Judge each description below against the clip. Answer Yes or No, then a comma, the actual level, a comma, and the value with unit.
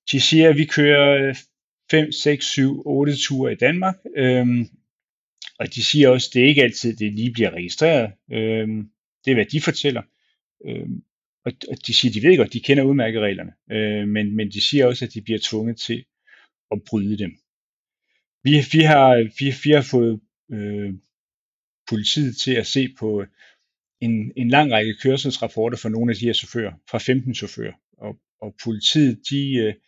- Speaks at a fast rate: No, average, 185 wpm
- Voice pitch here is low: Yes, low, 120 Hz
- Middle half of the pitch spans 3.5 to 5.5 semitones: Yes, average, 4.1 semitones